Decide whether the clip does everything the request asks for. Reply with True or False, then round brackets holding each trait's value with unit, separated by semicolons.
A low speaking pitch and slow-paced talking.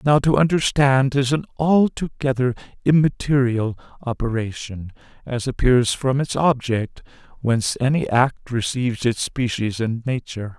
True (130 Hz; 120 wpm)